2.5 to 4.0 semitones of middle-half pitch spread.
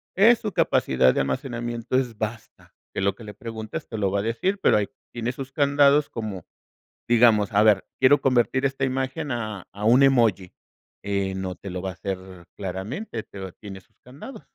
No: average, 5.1 semitones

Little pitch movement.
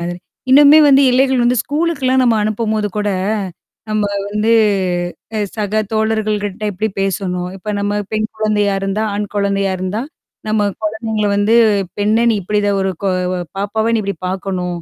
Yes: narrow, 1.9 semitones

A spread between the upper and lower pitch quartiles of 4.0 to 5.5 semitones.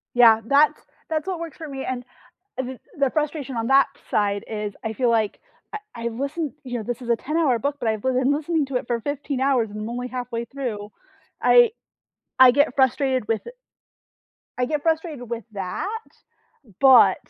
No: average, 3.6 semitones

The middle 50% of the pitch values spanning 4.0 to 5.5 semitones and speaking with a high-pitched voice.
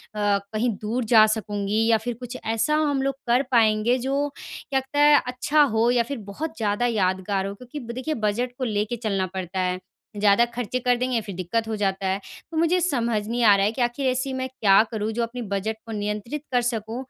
No: average, 3.5 semitones; high, 230 Hz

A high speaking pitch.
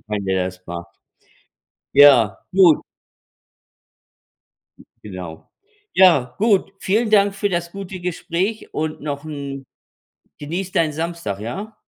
No: medium, 155 Hz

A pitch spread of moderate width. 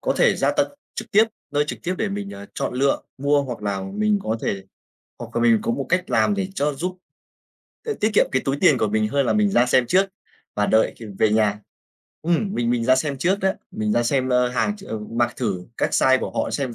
No: wide, 8.0 semitones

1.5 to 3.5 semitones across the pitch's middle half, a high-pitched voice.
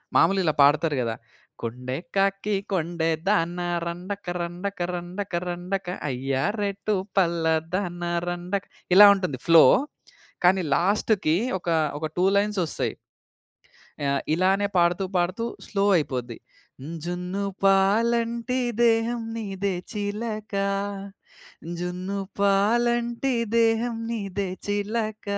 Yes: average, 3.2 semitones; high, 195 Hz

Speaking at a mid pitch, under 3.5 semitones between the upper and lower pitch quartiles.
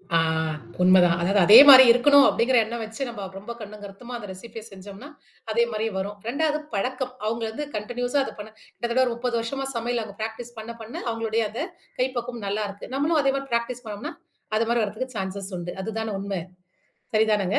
No: high, 225 Hz; average, 3.1 semitones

